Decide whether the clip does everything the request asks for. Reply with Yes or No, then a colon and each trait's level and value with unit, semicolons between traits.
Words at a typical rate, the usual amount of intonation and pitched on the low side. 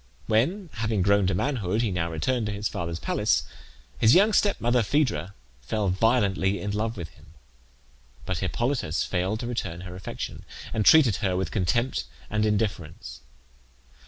Yes: average, 155 wpm; average, 4.5 semitones; low, 105 Hz